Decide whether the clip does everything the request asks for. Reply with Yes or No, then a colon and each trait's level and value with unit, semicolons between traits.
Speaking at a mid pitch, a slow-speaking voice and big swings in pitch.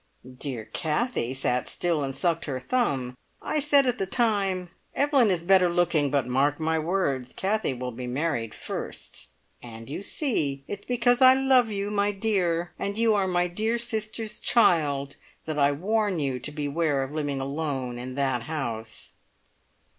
No: medium, 165 Hz; average, 165 wpm; wide, 7.2 semitones